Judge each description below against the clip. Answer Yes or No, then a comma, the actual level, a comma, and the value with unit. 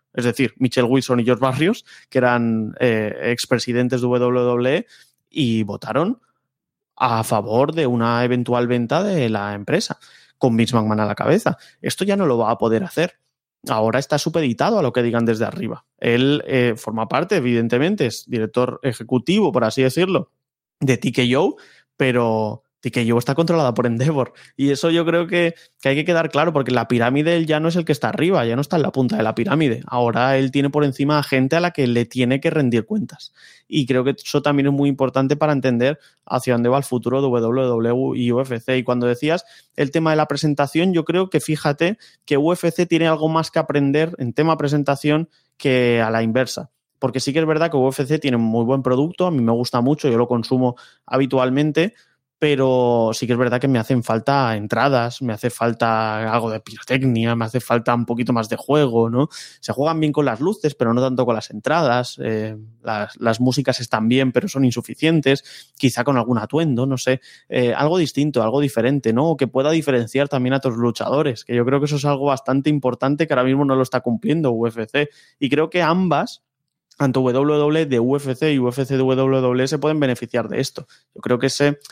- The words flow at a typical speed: No, fast, 205 wpm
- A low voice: Yes, low, 130 Hz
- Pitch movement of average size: Yes, average, 3.5 semitones